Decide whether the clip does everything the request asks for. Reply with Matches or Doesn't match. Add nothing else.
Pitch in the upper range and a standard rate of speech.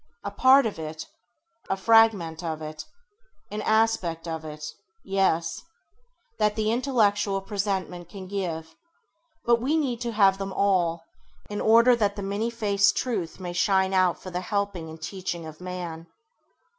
Matches